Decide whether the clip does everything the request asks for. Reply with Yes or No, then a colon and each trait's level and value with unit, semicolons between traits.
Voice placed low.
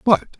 No: high, 215 Hz